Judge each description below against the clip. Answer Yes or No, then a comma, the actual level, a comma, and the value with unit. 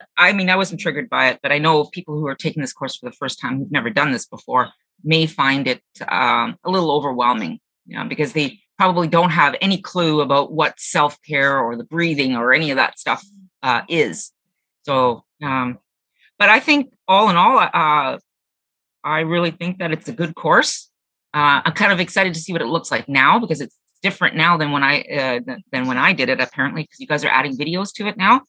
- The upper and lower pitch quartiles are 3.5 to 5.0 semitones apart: Yes, average, 4.4 semitones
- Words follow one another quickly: Yes, fast, 225 wpm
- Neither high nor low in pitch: Yes, medium, 155 Hz